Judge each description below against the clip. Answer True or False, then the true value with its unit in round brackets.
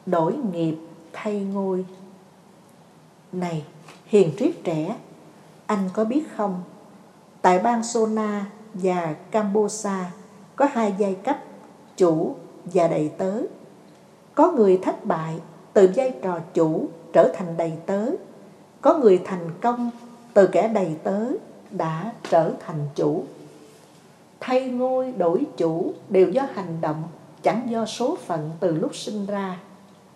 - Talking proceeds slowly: True (130 wpm)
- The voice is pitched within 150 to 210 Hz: True (190 Hz)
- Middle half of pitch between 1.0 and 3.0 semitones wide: False (3.7 semitones)